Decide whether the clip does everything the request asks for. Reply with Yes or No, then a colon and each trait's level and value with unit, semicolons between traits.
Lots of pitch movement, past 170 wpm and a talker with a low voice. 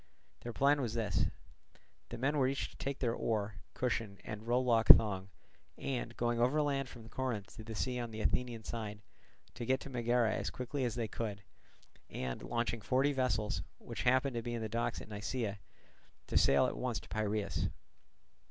No: average, 2.8 semitones; average, 185 wpm; low, 115 Hz